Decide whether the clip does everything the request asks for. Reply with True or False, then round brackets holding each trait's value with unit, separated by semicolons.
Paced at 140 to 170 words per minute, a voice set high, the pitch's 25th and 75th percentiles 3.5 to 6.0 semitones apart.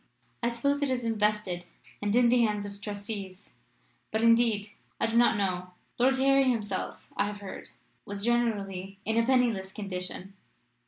False (160 wpm; 210 Hz; 3.1 semitones)